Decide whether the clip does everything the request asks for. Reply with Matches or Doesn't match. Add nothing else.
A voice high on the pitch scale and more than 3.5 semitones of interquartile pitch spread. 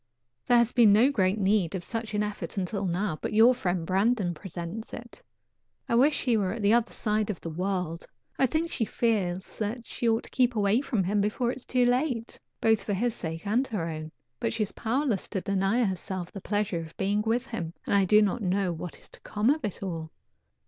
Matches